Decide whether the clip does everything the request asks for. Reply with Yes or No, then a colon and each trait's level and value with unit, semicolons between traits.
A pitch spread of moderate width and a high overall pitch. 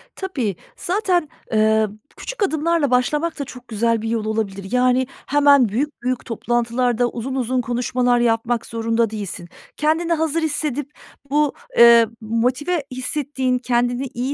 Yes: average, 4.2 semitones; very high, 250 Hz